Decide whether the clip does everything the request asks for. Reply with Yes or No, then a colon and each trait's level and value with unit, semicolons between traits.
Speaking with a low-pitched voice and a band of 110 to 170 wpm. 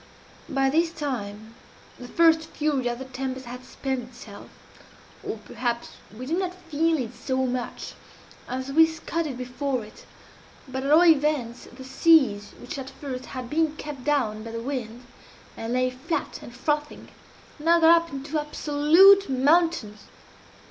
No: very high, 270 Hz; average, 155 wpm